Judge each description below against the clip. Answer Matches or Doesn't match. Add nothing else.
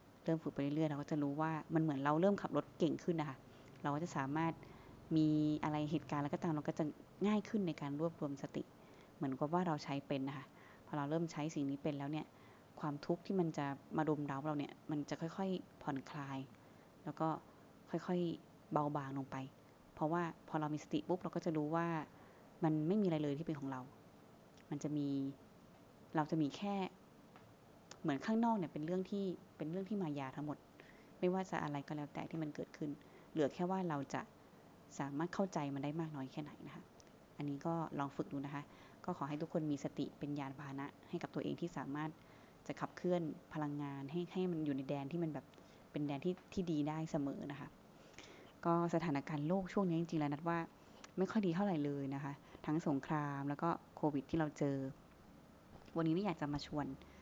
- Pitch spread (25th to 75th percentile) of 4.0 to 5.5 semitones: Doesn't match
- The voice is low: Doesn't match